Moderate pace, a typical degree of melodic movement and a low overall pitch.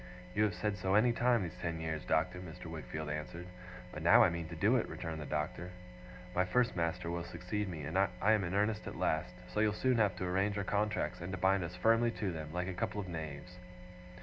No: fast, 230 wpm; average, 3.9 semitones; very low, 90 Hz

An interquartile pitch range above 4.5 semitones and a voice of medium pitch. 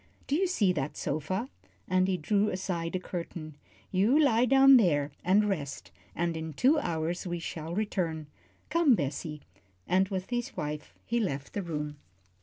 Yes: wide, 5.4 semitones; medium, 180 Hz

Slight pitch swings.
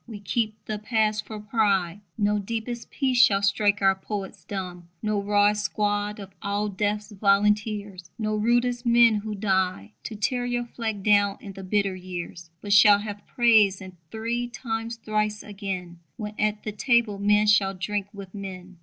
Yes: narrow, 1.7 semitones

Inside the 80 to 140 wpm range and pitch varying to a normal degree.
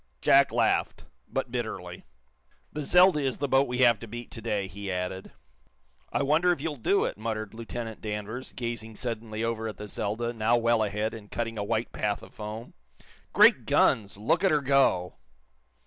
No: average, 180 wpm; average, 3.3 semitones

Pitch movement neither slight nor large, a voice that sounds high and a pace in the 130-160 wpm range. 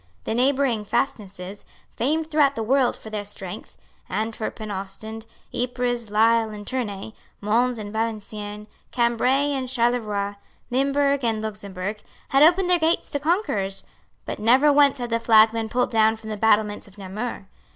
Yes: average, 3.8 semitones; high, 225 Hz; average, 155 wpm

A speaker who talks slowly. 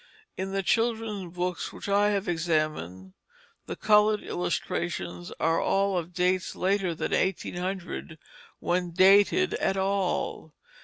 Yes: slow, 120 wpm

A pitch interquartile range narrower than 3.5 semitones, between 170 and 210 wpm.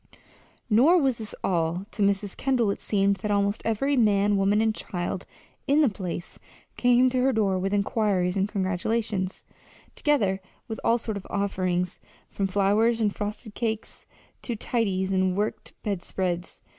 No: average, 2.9 semitones; average, 155 wpm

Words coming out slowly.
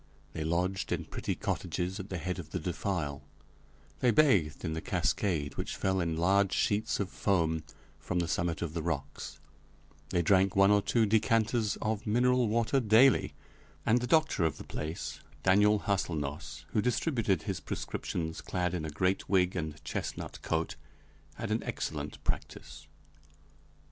No: average, 160 wpm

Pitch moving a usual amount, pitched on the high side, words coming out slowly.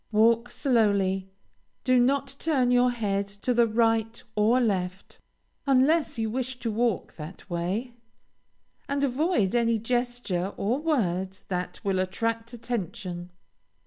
Yes: average, 4.2 semitones; high, 230 Hz; slow, 125 wpm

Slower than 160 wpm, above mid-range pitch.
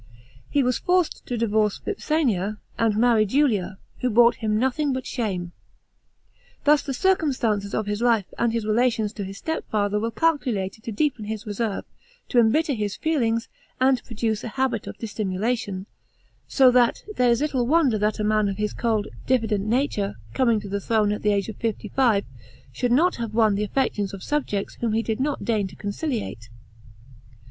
No: average, 180 wpm; high, 225 Hz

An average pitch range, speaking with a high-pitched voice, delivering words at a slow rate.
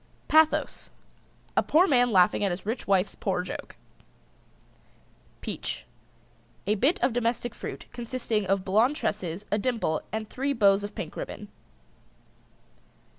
Yes: average, 4.0 semitones; high, 215 Hz; slow, 130 wpm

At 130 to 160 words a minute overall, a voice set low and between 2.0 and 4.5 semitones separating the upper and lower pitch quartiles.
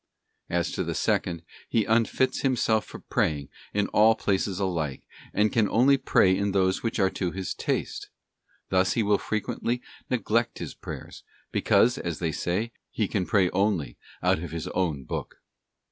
No: average, 175 wpm; low, 100 Hz; average, 4.1 semitones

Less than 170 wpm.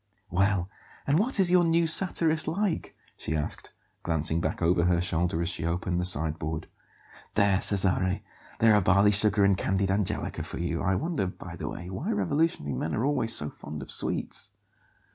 No: average, 180 wpm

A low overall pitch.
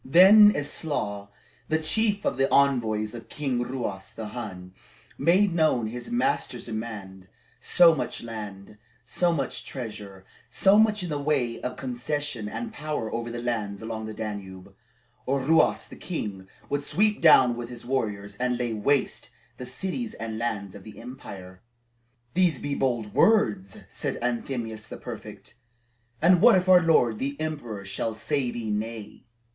Yes: low, 120 Hz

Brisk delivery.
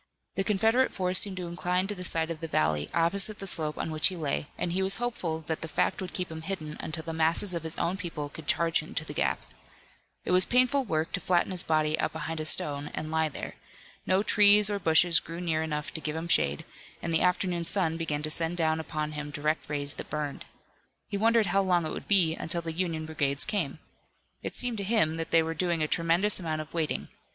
Yes: fast, 235 wpm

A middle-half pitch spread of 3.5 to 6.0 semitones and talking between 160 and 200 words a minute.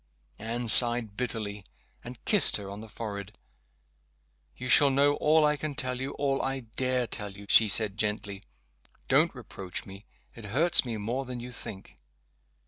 Yes: average, 4.2 semitones; average, 165 wpm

